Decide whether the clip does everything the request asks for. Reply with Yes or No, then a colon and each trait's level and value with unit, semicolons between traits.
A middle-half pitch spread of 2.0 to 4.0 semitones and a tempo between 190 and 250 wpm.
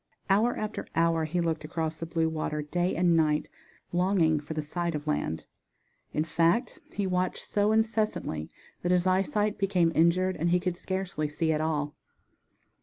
No: average, 3.0 semitones; average, 170 wpm